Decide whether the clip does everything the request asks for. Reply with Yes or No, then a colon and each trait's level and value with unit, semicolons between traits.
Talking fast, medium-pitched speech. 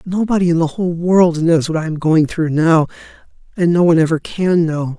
Yes: fast, 215 wpm; medium, 165 Hz